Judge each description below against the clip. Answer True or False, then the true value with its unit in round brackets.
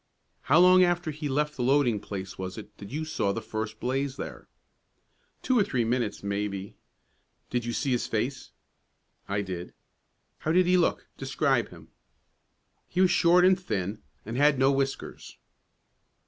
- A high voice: False (130 Hz)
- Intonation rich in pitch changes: True (7.0 semitones)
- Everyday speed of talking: True (160 wpm)